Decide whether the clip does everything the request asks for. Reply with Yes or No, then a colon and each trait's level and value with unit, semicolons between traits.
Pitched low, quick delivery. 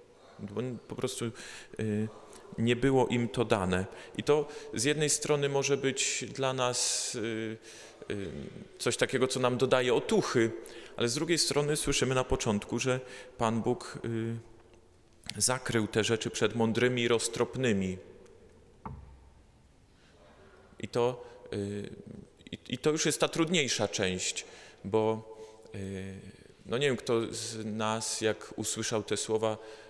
No: low, 115 Hz; average, 130 wpm